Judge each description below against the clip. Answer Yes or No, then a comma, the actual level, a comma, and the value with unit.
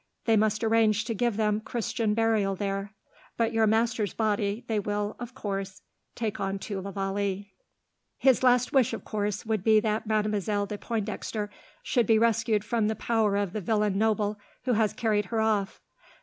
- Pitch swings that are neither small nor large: No, narrow, 1.8 semitones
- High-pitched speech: Yes, high, 215 Hz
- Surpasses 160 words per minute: Yes, average, 175 wpm